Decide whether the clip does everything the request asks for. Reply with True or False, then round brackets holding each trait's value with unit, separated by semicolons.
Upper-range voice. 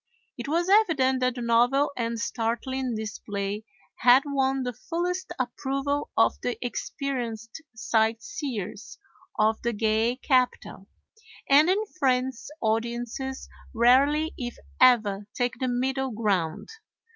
True (245 Hz)